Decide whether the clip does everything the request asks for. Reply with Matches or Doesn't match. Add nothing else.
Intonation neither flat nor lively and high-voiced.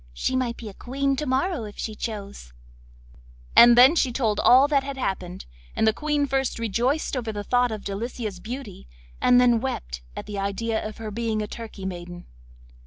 Matches